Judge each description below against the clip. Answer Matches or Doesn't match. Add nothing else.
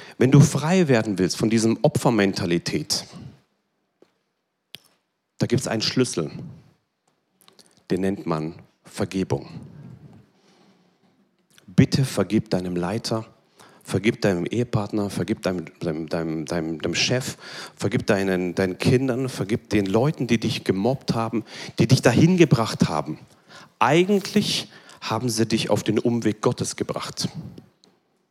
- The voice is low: Matches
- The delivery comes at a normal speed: Doesn't match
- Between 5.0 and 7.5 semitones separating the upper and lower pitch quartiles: Matches